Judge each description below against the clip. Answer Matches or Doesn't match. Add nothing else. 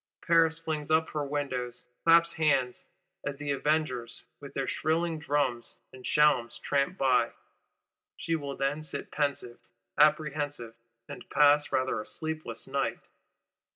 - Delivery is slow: Matches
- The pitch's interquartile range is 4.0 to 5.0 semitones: Doesn't match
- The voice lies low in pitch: Doesn't match